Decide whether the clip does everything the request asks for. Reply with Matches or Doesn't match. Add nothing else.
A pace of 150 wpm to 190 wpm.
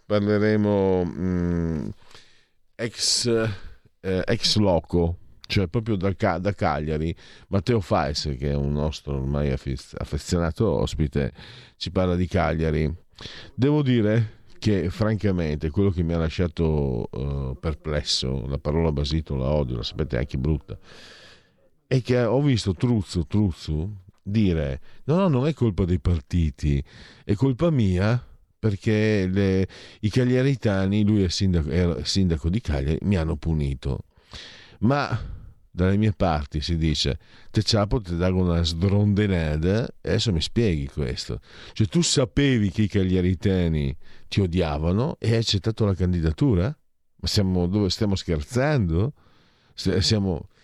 Doesn't match